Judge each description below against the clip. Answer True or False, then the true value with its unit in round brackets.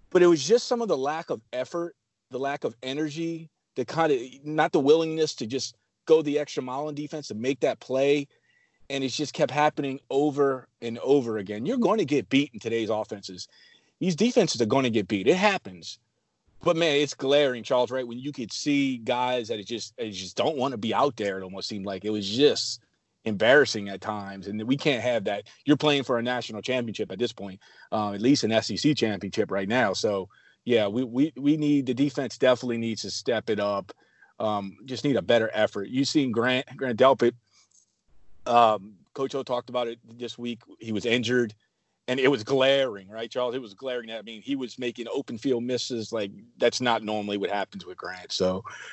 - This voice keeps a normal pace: False (215 wpm)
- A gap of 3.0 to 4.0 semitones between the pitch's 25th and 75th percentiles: False (4.4 semitones)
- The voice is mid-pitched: False (125 Hz)